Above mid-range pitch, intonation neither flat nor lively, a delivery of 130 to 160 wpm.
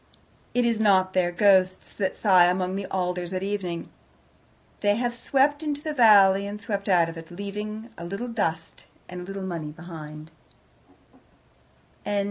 Yes: high, 195 Hz; average, 3.1 semitones; average, 155 wpm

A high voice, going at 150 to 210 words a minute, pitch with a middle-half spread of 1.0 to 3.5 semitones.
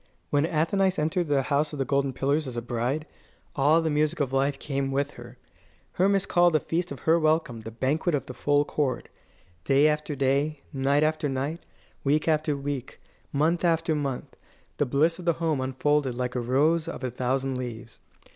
No: medium, 145 Hz; average, 190 wpm; average, 2.8 semitones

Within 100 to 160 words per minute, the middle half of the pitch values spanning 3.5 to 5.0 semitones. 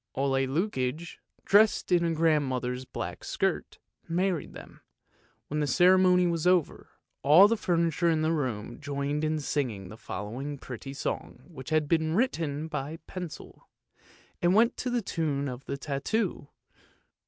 Yes: average, 150 wpm; average, 4.2 semitones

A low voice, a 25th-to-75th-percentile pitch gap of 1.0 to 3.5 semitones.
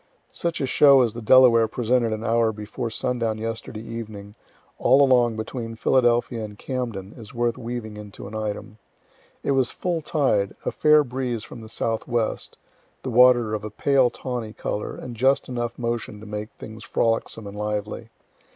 Yes: low, 115 Hz; narrow, 2.6 semitones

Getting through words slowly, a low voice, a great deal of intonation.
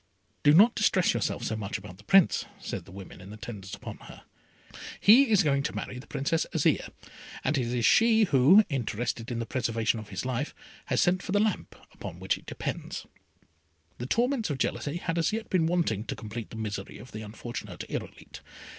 No: average, 200 wpm; low, 130 Hz; wide, 8.4 semitones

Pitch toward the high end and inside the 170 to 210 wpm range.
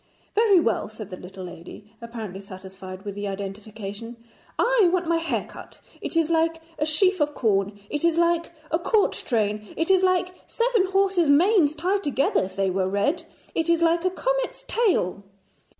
Yes: very high, 300 Hz; average, 180 wpm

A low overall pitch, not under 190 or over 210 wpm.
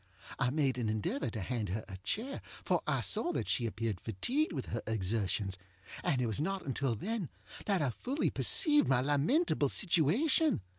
No: low, 130 Hz; average, 170 wpm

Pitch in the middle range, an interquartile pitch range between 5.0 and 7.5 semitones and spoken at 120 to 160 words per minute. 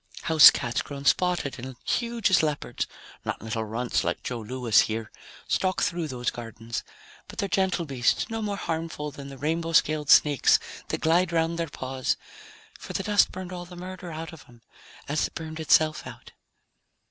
No: medium, 155 Hz; average, 5.3 semitones; average, 175 wpm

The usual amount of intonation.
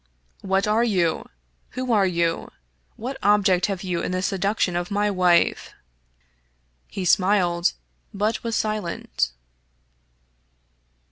Yes: average, 3.2 semitones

